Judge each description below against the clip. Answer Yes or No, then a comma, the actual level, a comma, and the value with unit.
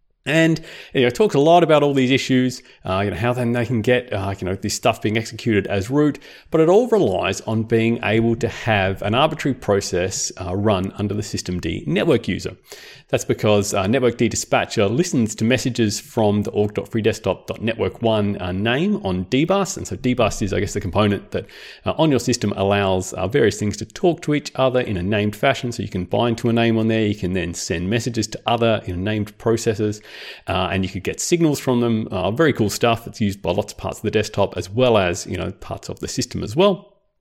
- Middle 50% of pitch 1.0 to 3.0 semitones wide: No, average, 4.2 semitones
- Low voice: Yes, low, 110 Hz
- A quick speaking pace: Yes, fast, 215 wpm